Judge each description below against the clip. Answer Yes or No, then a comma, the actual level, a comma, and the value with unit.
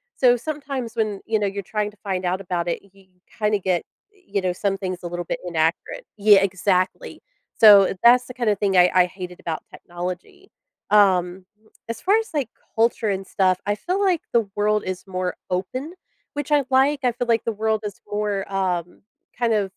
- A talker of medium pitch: No, high, 205 Hz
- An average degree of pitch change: Yes, average, 4.3 semitones